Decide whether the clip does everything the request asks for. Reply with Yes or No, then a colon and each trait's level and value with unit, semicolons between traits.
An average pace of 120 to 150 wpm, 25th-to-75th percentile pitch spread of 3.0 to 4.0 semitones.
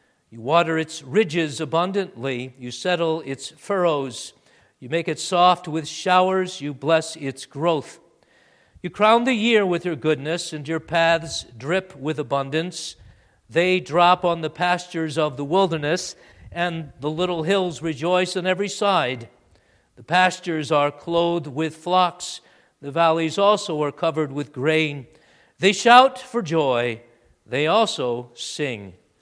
Yes: average, 140 wpm; average, 3.7 semitones